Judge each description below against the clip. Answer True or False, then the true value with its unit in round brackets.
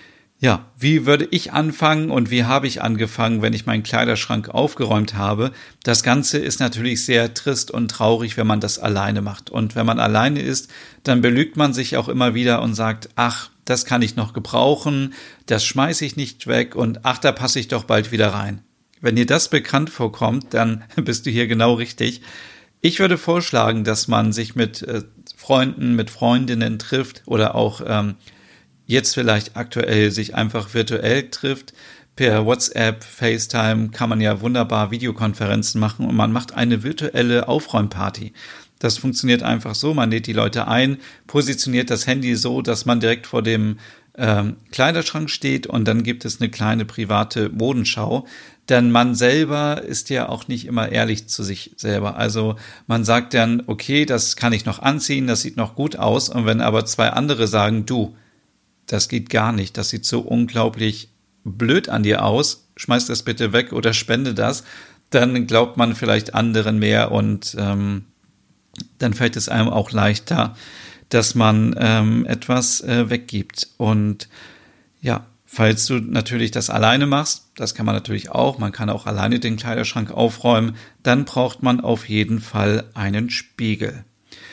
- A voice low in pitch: True (115 Hz)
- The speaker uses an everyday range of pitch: False (2.2 semitones)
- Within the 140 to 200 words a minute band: True (170 wpm)